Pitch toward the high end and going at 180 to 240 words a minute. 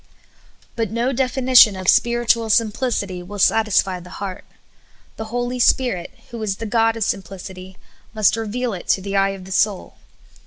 No: high, 215 Hz; average, 165 wpm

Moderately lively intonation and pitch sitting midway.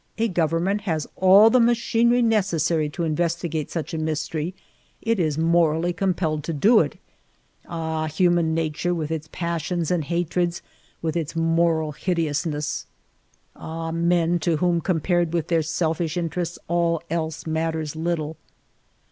No: narrow, 1.8 semitones; medium, 165 Hz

